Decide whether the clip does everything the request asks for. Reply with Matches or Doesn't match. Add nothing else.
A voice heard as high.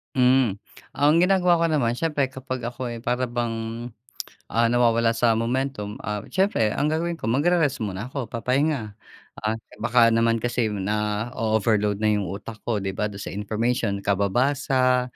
Doesn't match